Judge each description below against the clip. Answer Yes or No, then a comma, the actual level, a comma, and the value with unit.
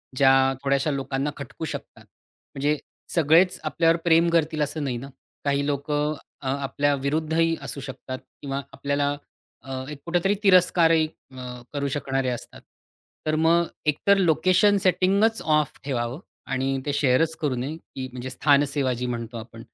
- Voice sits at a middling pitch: Yes, medium, 145 Hz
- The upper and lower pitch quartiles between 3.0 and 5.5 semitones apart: Yes, average, 3.3 semitones